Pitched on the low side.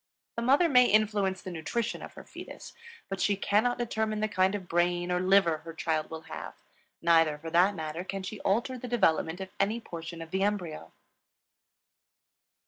No: high, 190 Hz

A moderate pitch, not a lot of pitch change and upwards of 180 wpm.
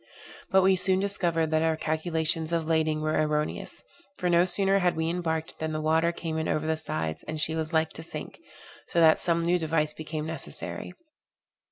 Yes: medium, 160 Hz; narrow, 1.6 semitones; average, 195 wpm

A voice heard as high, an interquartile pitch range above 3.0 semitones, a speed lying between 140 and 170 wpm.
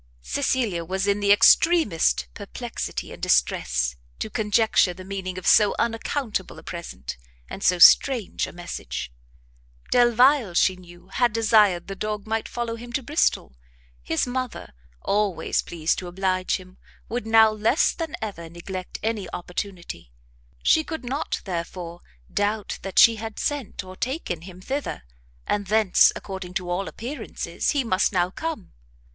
Yes: high, 200 Hz; average, 4.4 semitones; average, 150 wpm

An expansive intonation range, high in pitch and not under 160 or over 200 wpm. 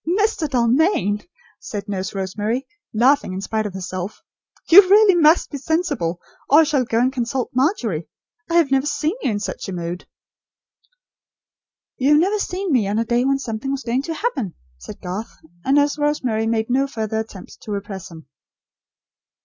Yes: wide, 6.3 semitones; high, 245 Hz; average, 180 wpm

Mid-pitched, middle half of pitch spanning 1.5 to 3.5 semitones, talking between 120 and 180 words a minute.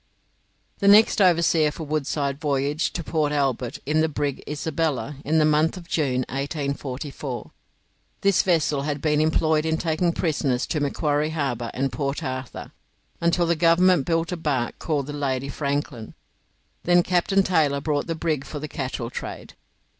Yes: medium, 150 Hz; average, 2.8 semitones; average, 160 wpm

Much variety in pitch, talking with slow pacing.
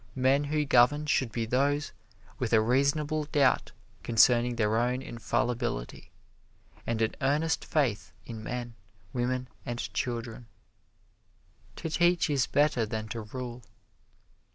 No: average, 3.5 semitones; slow, 125 wpm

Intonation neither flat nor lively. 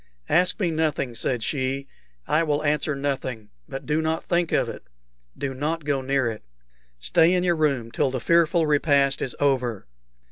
Yes: average, 3.4 semitones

